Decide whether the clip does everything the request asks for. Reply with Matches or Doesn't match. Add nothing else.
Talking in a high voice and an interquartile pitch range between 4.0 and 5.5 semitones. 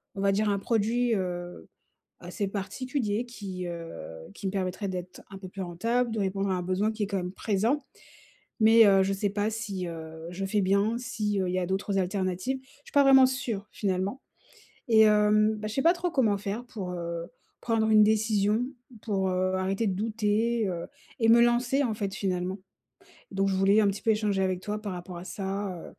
Doesn't match